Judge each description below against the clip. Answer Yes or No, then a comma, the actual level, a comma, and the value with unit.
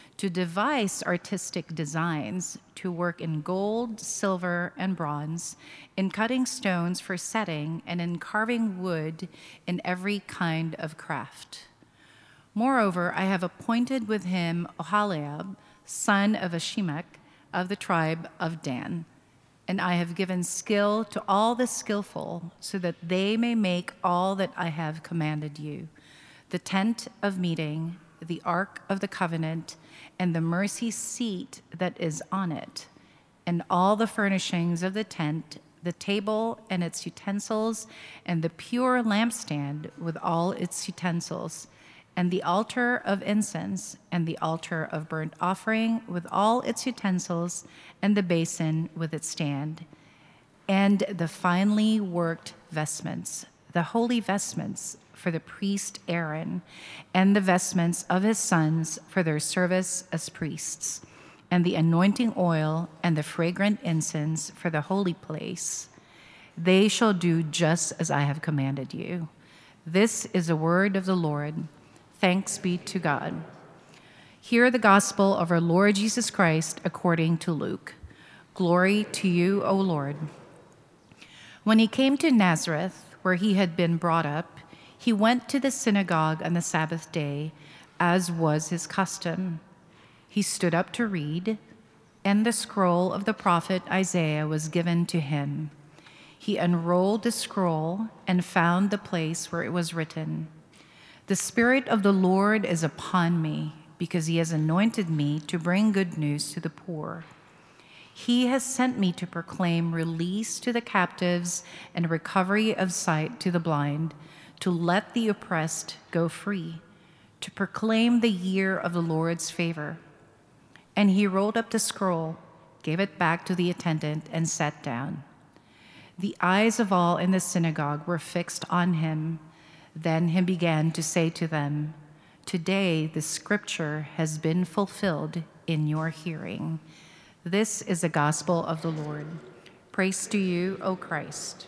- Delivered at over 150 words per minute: No, average, 145 wpm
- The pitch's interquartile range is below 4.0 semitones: Yes, average, 3.3 semitones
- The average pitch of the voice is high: No, medium, 175 Hz